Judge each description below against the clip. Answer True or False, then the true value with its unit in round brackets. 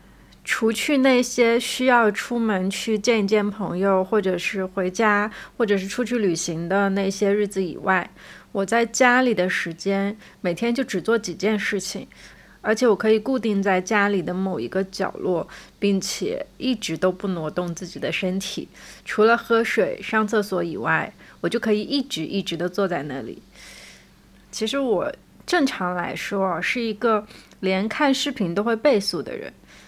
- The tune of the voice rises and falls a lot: False (3.5 semitones)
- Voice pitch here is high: True (205 Hz)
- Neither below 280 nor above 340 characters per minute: False (240 characters per minute)